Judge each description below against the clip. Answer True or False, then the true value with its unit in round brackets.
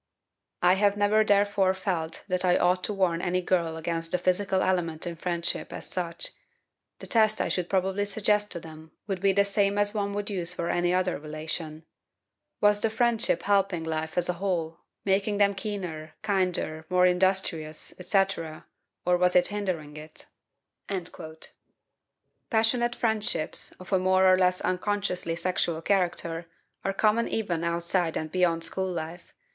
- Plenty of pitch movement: False (3.0 semitones)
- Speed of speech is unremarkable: True (160 wpm)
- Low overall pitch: False (185 Hz)